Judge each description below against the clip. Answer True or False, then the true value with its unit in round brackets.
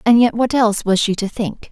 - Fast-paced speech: True (280 wpm)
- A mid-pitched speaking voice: False (220 Hz)